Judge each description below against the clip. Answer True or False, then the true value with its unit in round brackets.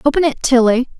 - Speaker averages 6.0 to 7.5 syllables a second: True (6.1 syllables/s)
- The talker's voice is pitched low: False (265 Hz)